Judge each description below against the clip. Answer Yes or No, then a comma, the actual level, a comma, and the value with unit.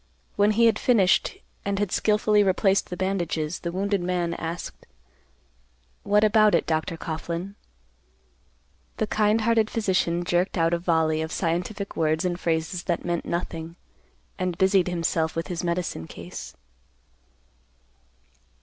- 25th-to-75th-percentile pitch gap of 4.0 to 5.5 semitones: No, average, 3.2 semitones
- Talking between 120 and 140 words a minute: Yes, slow, 135 wpm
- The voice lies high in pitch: No, medium, 180 Hz